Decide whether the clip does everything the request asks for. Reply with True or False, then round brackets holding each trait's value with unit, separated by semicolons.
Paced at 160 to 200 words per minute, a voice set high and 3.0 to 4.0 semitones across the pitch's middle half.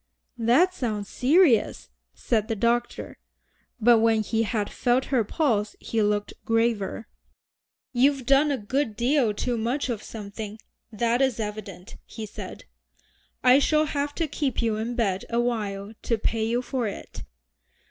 False (145 wpm; 230 Hz; 3.3 semitones)